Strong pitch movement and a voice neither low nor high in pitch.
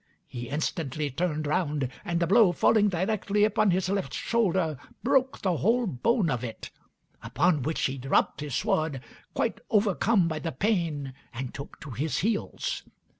Yes: wide, 6.2 semitones; medium, 170 Hz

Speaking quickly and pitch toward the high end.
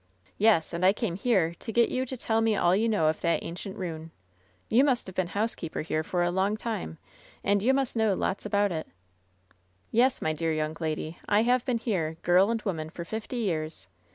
Yes: fast, 210 wpm; high, 195 Hz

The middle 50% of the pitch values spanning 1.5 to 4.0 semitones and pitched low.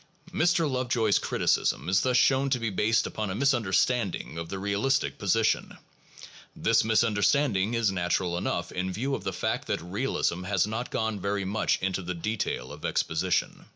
No: average, 4.4 semitones; low, 105 Hz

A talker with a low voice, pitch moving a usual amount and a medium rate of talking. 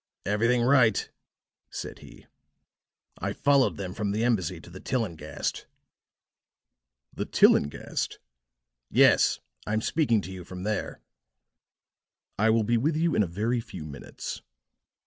No: low, 110 Hz; average, 4.5 semitones; slow, 125 wpm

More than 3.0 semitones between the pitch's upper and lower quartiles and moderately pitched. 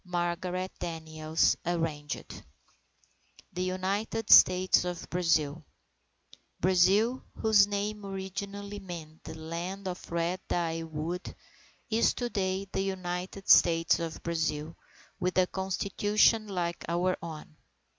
No: average, 2.7 semitones; medium, 180 Hz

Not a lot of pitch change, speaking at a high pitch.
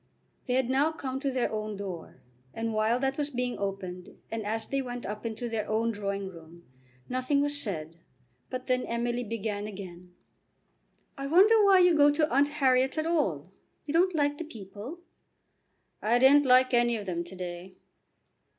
No: wide, 5.6 semitones; high, 240 Hz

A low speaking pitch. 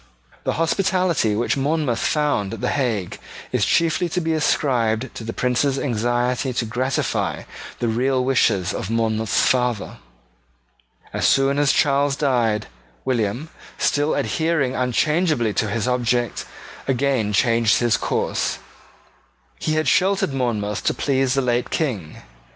Yes: low, 125 Hz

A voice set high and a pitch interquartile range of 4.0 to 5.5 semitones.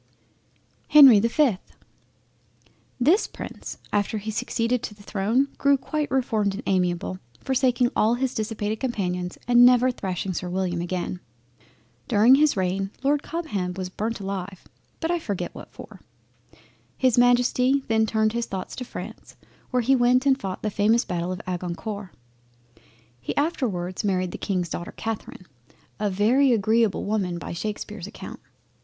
Yes: high, 215 Hz; average, 5.0 semitones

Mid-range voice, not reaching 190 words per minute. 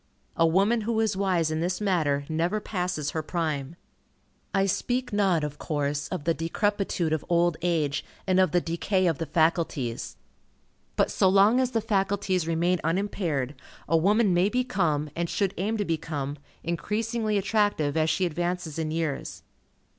Yes: medium, 175 Hz; average, 160 wpm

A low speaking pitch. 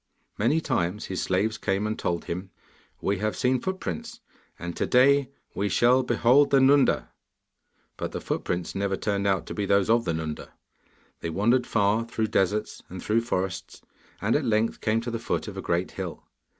Yes: low, 105 Hz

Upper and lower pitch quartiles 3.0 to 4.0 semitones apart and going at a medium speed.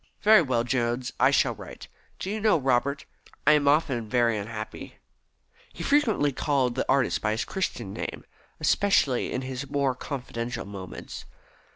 Yes: average, 3.6 semitones; average, 160 wpm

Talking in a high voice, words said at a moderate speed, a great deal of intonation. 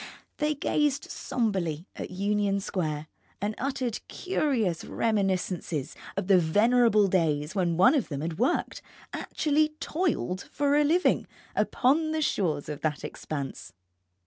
No: high, 205 Hz; slow, 130 wpm; wide, 8.7 semitones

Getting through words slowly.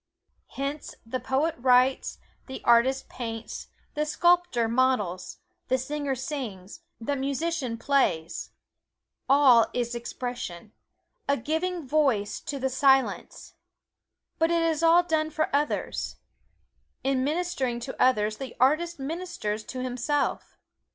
Yes: slow, 115 wpm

